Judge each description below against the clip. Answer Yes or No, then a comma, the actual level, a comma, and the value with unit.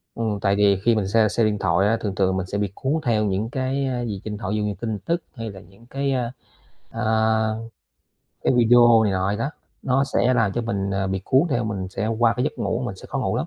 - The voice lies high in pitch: No, low, 110 Hz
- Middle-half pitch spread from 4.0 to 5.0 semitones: No, average, 3.3 semitones